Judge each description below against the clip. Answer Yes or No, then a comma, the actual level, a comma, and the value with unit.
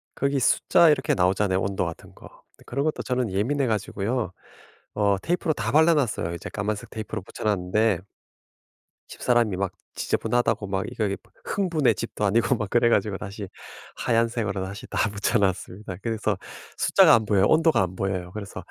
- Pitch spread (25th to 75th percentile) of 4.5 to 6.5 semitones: No, average, 3.8 semitones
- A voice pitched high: No, low, 105 Hz